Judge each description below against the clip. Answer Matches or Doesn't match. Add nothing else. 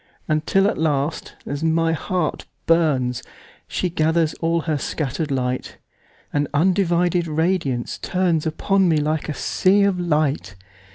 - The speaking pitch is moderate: Matches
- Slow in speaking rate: Matches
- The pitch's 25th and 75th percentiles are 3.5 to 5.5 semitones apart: Doesn't match